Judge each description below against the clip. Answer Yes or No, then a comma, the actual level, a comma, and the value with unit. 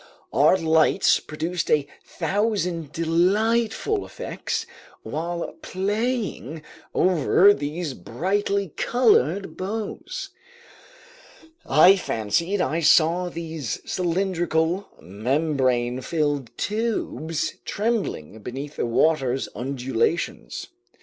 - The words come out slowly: Yes, slow, 80 wpm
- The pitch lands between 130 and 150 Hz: No, medium, 165 Hz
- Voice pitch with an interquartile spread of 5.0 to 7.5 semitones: Yes, wide, 5.4 semitones